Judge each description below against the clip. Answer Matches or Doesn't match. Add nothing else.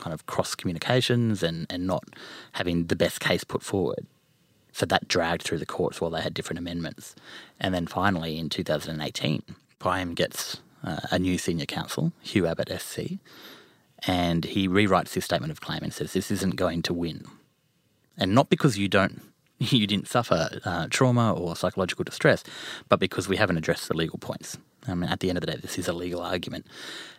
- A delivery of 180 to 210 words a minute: Matches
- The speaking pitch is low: Matches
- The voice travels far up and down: Doesn't match